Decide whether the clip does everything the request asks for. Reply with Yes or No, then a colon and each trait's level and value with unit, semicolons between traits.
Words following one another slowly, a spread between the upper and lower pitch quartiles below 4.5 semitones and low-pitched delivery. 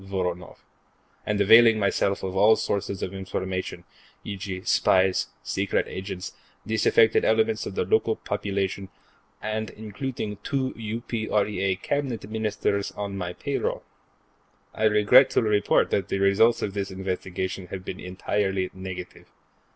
Yes: slow, 125 wpm; narrow, 2.5 semitones; low, 100 Hz